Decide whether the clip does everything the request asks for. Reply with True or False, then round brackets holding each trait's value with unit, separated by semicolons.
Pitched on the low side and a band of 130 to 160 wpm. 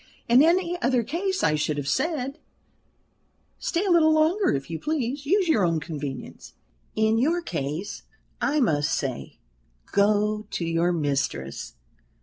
False (220 Hz; 140 wpm)